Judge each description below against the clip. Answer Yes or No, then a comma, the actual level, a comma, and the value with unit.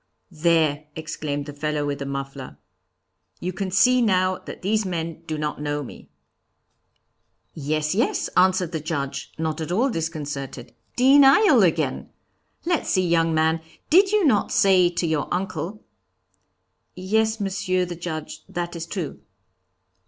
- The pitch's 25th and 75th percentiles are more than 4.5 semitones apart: No, average, 4.0 semitones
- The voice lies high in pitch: No, medium, 170 Hz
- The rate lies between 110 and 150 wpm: Yes, average, 145 wpm